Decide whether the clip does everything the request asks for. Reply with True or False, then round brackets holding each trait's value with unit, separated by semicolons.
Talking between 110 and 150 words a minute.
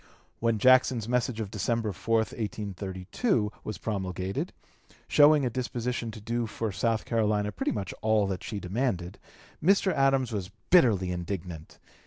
True (140 wpm)